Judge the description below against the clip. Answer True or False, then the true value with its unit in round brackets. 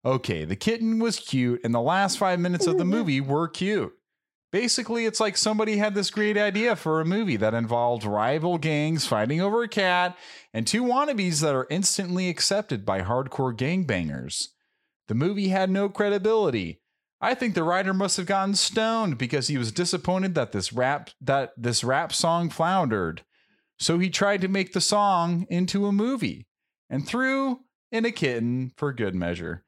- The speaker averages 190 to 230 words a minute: False (175 wpm)